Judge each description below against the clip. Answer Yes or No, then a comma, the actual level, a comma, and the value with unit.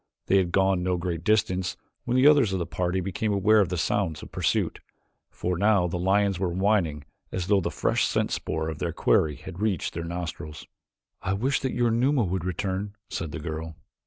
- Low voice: Yes, very low, 95 Hz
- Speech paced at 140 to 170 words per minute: No, fast, 205 wpm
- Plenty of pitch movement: No, average, 3.2 semitones